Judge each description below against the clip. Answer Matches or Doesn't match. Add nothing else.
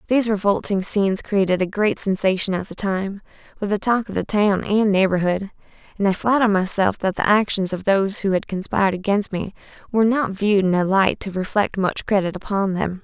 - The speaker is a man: Doesn't match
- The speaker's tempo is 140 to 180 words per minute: Doesn't match